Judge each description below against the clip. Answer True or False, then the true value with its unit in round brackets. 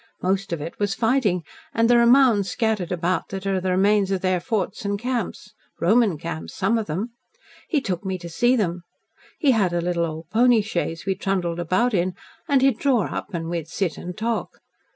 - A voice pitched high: True (195 Hz)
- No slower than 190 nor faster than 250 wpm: True (205 wpm)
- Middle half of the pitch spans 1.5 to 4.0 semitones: False (4.7 semitones)